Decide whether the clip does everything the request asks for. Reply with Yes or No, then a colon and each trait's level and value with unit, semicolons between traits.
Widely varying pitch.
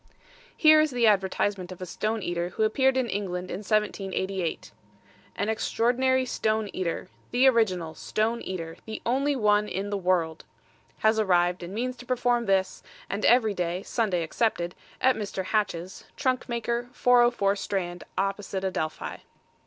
No: average, 4.4 semitones